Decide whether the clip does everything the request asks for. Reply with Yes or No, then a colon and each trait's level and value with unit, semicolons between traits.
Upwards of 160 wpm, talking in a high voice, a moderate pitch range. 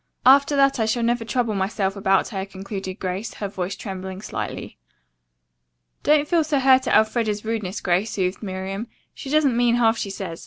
Yes: average, 180 wpm; high, 215 Hz; average, 4.1 semitones